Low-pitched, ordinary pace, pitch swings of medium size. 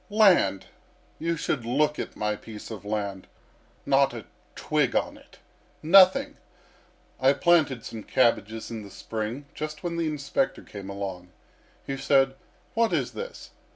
No: low, 130 Hz; average, 145 wpm; wide, 6.5 semitones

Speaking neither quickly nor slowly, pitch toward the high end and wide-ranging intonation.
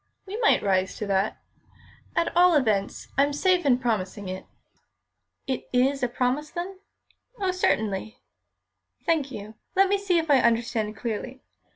Yes: average, 150 wpm; very high, 255 Hz; wide, 7.8 semitones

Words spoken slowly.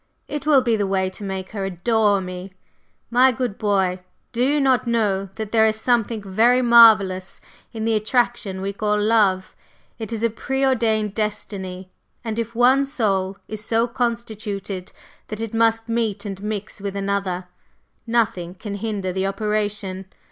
No: average, 160 wpm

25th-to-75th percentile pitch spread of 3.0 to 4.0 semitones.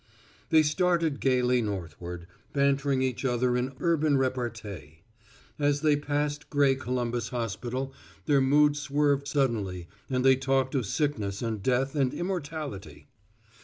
Yes: average, 3.3 semitones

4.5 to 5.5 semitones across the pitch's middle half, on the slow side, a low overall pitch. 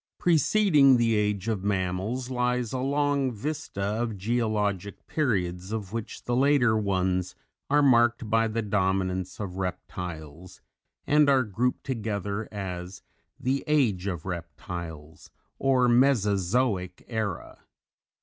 Yes: average, 5.1 semitones; slow, 120 wpm; low, 110 Hz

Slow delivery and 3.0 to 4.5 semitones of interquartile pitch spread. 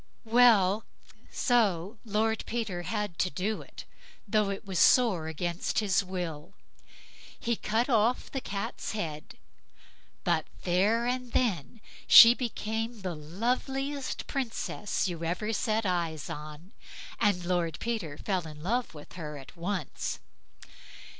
No: slow, 125 wpm; average, 4.9 semitones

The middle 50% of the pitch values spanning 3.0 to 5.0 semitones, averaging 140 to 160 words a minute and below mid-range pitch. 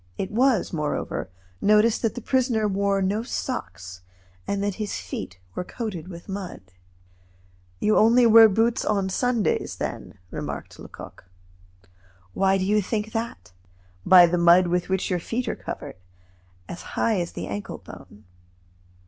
No: average, 3.9 semitones; average, 150 wpm; high, 200 Hz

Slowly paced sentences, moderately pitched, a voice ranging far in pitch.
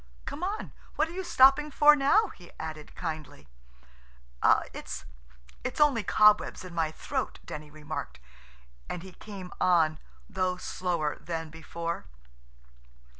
Yes: slow, 125 wpm; medium, 180 Hz; wide, 8.7 semitones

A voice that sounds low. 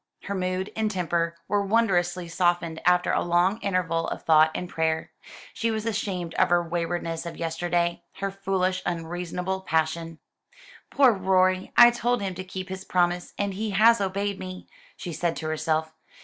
No: medium, 180 Hz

